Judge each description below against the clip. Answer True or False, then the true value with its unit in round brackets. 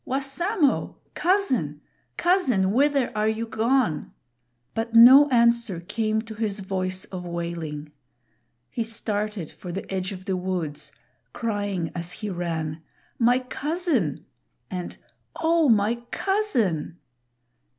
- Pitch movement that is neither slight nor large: False (6.0 semitones)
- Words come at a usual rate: False (115 wpm)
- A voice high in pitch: True (215 Hz)